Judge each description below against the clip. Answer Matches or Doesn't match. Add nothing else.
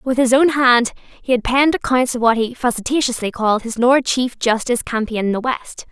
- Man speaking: Doesn't match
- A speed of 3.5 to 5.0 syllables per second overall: Doesn't match